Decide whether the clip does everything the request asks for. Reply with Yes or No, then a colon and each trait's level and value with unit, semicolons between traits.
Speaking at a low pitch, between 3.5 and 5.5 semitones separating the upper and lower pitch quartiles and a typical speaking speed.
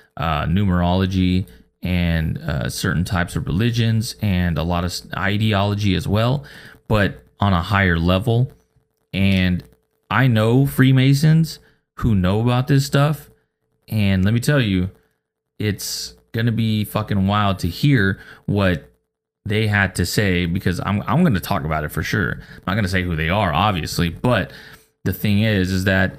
Yes: low, 100 Hz; average, 4.0 semitones; average, 165 wpm